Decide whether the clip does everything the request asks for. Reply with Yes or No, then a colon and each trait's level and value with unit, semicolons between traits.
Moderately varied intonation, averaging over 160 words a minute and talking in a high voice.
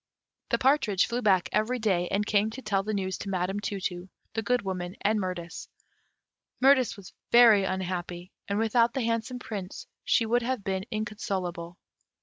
Yes: average, 3.5 semitones; average, 170 wpm; high, 205 Hz